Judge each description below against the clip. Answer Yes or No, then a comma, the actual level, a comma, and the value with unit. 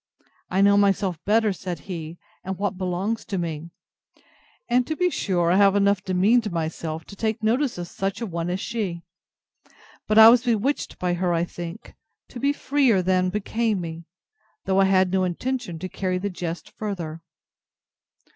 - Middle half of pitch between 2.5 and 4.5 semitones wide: Yes, average, 3.8 semitones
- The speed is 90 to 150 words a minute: No, average, 175 wpm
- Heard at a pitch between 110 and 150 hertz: No, high, 190 Hz